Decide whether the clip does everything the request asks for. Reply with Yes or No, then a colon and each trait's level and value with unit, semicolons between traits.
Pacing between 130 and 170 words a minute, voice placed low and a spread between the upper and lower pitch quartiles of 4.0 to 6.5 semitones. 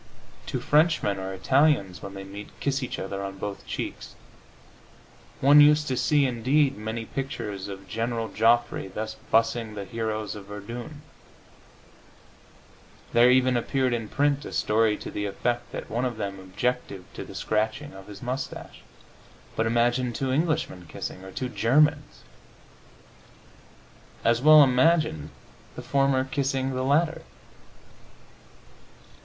Yes: slow, 135 wpm; low, 120 Hz; average, 4.7 semitones